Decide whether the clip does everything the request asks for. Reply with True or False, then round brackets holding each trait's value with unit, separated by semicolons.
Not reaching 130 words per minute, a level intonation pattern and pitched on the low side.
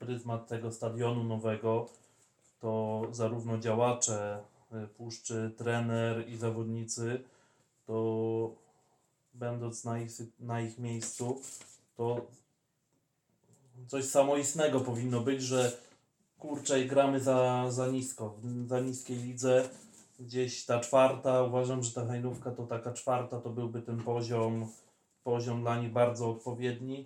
True (115 wpm; 1.8 semitones; 120 Hz)